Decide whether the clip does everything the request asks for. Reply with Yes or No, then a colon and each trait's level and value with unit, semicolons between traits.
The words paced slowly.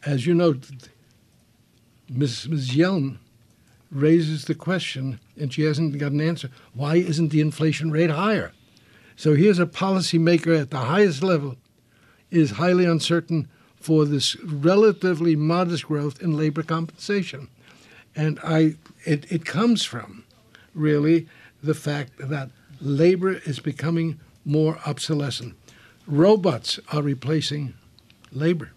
Yes: slow, 120 wpm